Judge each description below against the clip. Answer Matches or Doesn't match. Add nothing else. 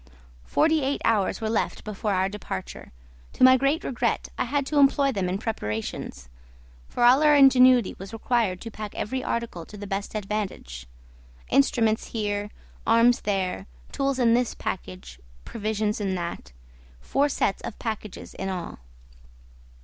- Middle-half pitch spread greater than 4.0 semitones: Matches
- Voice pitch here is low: Doesn't match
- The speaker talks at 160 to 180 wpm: Doesn't match